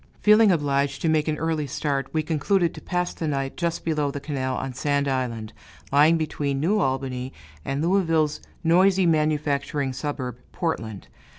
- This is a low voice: No, medium, 145 Hz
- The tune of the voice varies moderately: Yes, average, 3.2 semitones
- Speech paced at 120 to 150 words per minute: No, average, 160 wpm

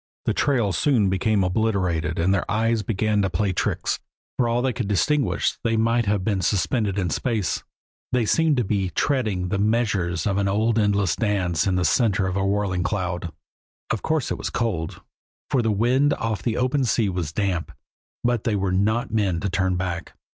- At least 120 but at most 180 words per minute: No, average, 190 wpm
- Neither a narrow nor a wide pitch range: Yes, average, 3.7 semitones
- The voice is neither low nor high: No, low, 105 Hz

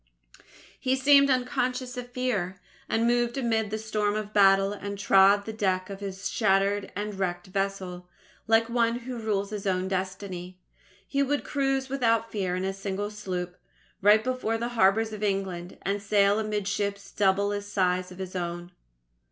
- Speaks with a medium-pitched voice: No, high, 205 Hz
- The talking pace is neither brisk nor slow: Yes, average, 170 wpm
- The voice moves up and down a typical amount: Yes, average, 3.0 semitones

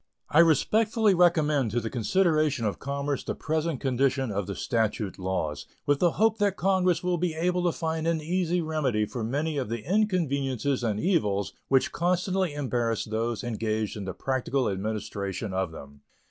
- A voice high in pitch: No, medium, 140 Hz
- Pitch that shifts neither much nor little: No, wide, 7.7 semitones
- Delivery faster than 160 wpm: Yes, average, 170 wpm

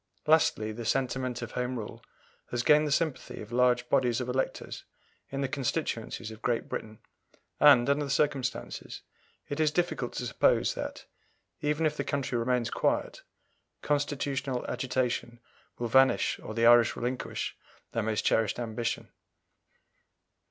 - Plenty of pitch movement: No, average, 3.0 semitones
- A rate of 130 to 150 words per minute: Yes, average, 145 wpm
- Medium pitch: No, low, 125 Hz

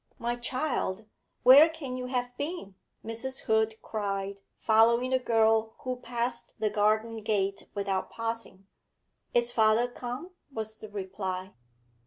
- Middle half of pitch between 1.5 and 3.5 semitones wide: Yes, average, 2.8 semitones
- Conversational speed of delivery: No, slow, 130 wpm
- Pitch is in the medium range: No, high, 225 Hz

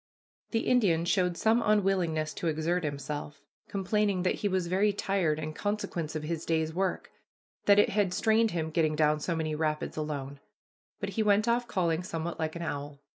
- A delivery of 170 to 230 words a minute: Yes, average, 180 wpm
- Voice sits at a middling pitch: Yes, medium, 170 Hz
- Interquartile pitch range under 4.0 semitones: No, average, 4.4 semitones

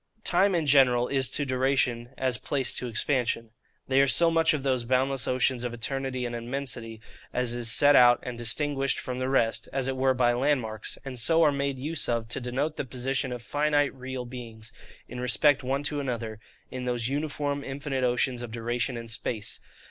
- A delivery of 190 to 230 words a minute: Yes, average, 195 wpm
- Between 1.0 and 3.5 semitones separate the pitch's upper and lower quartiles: Yes, narrow, 2.5 semitones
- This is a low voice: Yes, low, 130 Hz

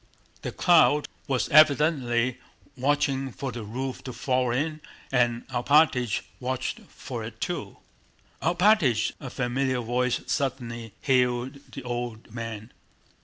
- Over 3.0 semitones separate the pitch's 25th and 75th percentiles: No, narrow, 2.6 semitones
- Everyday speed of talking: No, slow, 120 wpm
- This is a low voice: Yes, low, 125 Hz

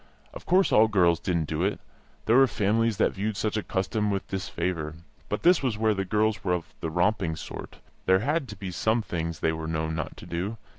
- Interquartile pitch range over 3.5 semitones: Yes, average, 4.4 semitones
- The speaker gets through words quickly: Yes, fast, 225 wpm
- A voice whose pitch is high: No, low, 100 Hz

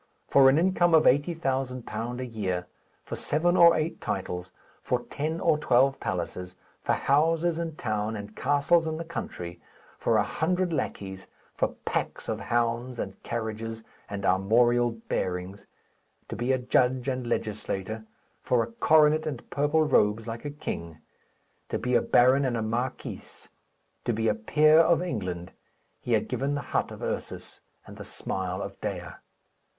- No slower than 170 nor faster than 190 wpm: No, average, 160 wpm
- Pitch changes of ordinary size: No, wide, 6.1 semitones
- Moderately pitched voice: No, low, 120 Hz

